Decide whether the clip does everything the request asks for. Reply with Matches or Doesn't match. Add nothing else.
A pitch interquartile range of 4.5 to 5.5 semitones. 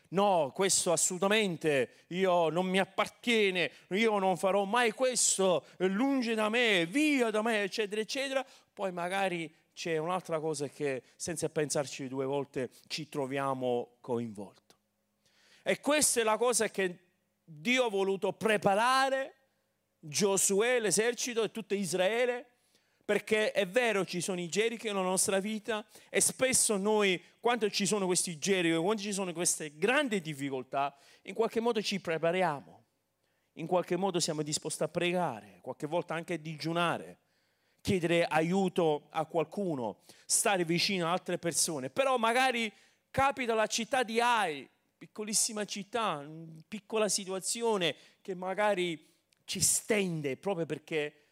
Matches